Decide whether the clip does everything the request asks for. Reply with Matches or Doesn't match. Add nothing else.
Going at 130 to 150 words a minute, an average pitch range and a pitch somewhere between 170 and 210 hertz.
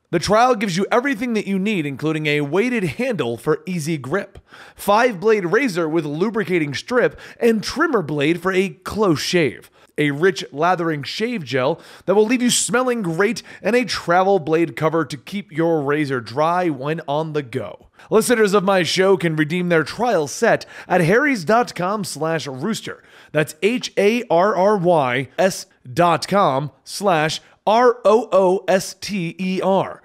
Matches